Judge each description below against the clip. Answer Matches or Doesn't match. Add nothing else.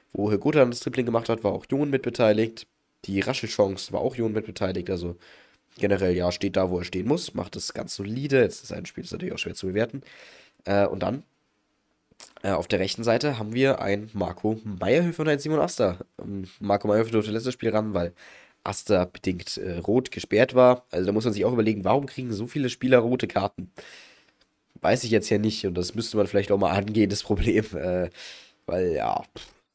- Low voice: Matches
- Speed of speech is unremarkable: Doesn't match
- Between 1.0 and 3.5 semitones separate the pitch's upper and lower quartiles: Doesn't match